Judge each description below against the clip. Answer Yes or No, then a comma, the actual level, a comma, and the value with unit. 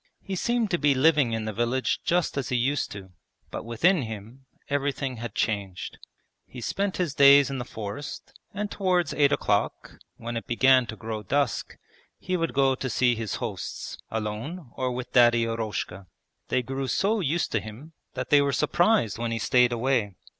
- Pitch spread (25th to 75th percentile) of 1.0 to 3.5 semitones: No, average, 4.4 semitones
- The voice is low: Yes, low, 130 Hz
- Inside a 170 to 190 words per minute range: Yes, average, 180 wpm